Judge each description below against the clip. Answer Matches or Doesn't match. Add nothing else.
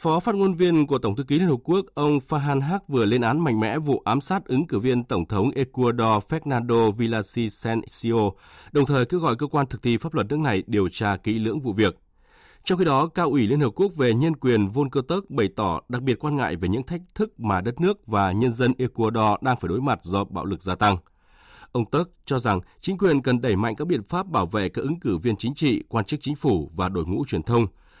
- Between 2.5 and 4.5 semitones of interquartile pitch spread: Doesn't match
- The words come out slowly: Doesn't match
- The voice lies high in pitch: Doesn't match